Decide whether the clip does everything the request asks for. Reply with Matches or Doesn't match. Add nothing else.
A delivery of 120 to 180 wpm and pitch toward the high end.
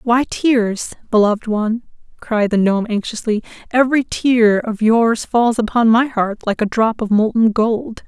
Matches